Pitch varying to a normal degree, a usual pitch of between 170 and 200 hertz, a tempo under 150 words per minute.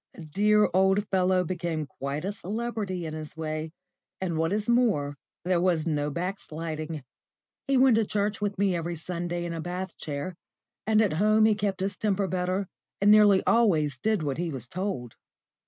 No: average, 4.4 semitones; medium, 185 Hz; average, 180 wpm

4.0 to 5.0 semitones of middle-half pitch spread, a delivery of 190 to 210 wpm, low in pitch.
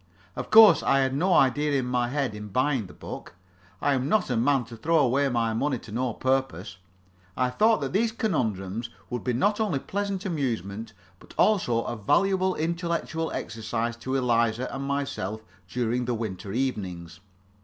No: average, 4.6 semitones; average, 175 wpm; low, 130 Hz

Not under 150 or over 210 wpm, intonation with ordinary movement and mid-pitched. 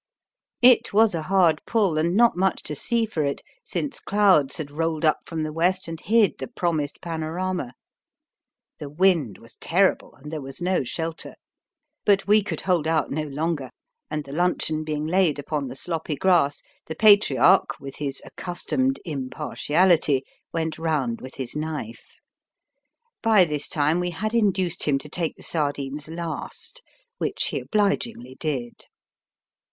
Yes: average, 155 wpm; average, 4.1 semitones; medium, 160 Hz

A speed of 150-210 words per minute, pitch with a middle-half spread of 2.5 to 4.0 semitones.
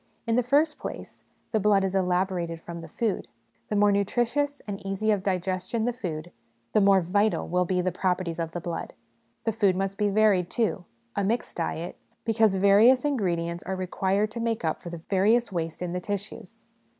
Yes: average, 190 wpm; average, 3.4 semitones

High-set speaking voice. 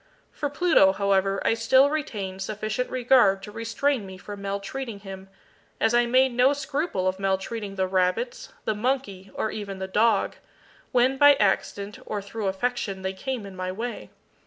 Yes: high, 210 Hz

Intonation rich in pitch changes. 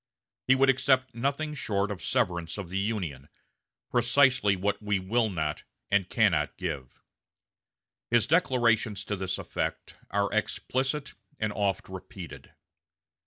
No: average, 5.0 semitones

